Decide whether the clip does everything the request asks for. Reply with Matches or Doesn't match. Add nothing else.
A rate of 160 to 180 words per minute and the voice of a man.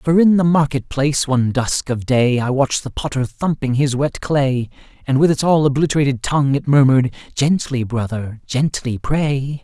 Matches